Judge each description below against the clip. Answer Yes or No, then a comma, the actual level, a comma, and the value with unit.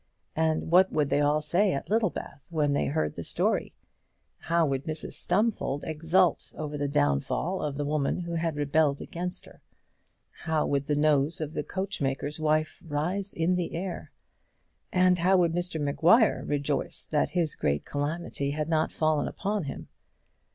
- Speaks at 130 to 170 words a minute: Yes, average, 165 wpm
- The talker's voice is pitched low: No, medium, 155 Hz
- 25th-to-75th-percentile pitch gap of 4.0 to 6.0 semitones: No, average, 3.2 semitones